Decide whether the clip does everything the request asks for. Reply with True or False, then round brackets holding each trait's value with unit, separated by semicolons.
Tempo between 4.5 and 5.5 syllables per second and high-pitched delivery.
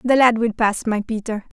True (5.1 syllables/s; 225 Hz)